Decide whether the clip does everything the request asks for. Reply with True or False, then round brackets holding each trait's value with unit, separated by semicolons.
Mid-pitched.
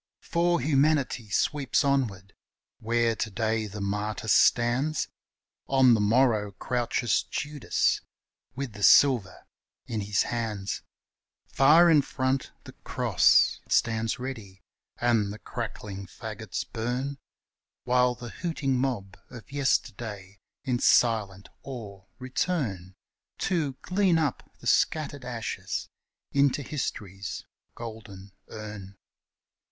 False (120 Hz)